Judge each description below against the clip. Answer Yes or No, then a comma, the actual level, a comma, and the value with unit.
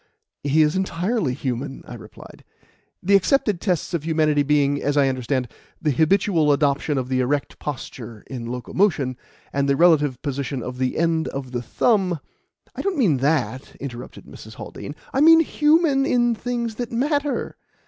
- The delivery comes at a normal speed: Yes, average, 165 wpm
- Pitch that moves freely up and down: Yes, wide, 7.0 semitones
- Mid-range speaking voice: Yes, medium, 150 Hz